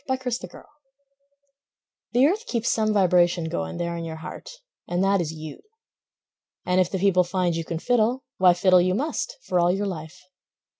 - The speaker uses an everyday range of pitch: Yes, average, 3.9 semitones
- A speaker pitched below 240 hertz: Yes, medium, 185 Hz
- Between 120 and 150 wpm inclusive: No, average, 180 wpm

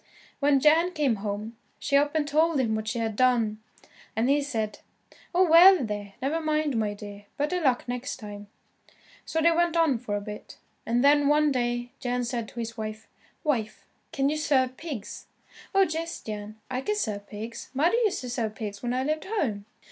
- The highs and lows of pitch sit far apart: Yes, wide, 5.8 semitones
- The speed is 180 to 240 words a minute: Yes, average, 195 wpm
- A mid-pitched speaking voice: No, very high, 255 Hz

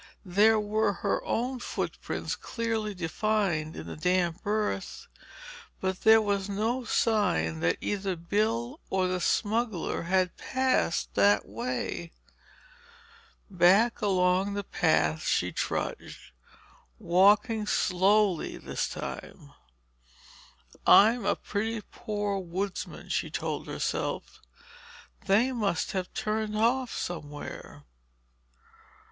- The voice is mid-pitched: No, high, 200 Hz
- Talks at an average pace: No, slow, 100 wpm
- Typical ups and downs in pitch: Yes, average, 3.6 semitones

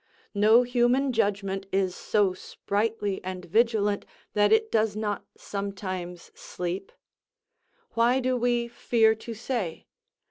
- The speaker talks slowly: Yes, slow, 115 wpm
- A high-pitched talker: Yes, high, 210 Hz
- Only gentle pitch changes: No, average, 3.3 semitones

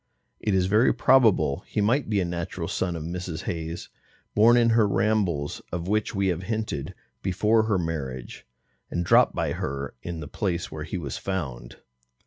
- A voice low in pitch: Yes, very low, 90 Hz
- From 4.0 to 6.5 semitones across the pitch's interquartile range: Yes, average, 4.7 semitones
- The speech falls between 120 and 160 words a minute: No, average, 175 wpm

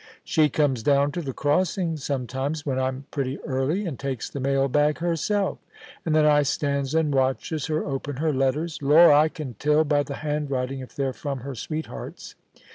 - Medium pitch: Yes, medium, 145 Hz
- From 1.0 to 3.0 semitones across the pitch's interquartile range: Yes, narrow, 2.4 semitones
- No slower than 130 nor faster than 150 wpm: No, average, 195 wpm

